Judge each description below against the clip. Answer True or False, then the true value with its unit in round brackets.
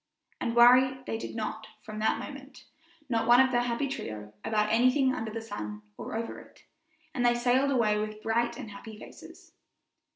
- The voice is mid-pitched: False (230 Hz)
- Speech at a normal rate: True (185 wpm)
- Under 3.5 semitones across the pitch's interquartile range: True (2.4 semitones)